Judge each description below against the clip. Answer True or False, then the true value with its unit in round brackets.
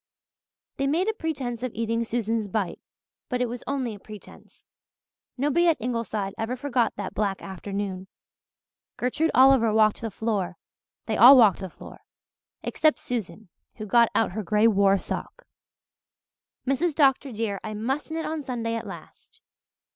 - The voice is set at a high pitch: True (230 Hz)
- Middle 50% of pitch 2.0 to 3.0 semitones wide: False (4.2 semitones)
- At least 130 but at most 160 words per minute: True (155 wpm)